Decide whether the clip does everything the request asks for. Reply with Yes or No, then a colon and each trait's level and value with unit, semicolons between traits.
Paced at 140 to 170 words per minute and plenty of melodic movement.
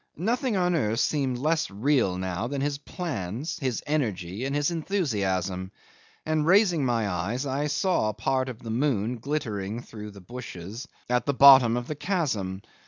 Yes: average, 165 wpm; wide, 6.1 semitones